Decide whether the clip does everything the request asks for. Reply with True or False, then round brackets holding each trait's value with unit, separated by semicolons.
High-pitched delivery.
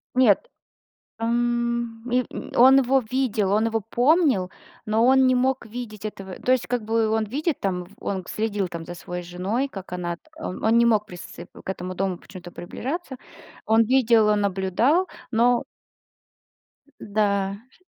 True (225 Hz)